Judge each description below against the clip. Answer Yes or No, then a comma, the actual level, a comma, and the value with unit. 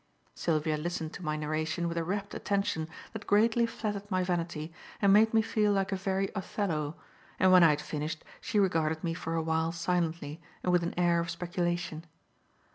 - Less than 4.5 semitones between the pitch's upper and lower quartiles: Yes, average, 3.4 semitones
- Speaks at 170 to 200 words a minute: Yes, average, 190 wpm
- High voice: No, medium, 175 Hz